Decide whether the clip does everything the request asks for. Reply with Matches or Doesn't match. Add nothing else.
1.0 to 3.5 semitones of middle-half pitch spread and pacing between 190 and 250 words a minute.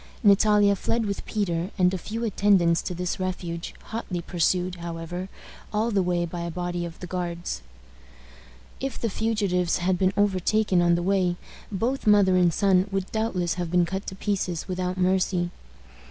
Doesn't match